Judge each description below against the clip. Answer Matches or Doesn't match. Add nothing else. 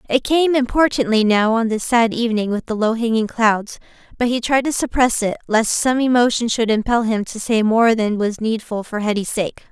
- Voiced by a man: Doesn't match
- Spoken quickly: Matches